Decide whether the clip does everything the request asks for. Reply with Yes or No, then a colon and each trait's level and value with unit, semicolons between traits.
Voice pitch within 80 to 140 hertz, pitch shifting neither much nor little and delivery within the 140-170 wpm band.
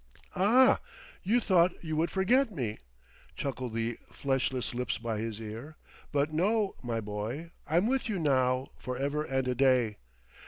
No: low, 135 Hz; wide, 6.6 semitones; average, 155 wpm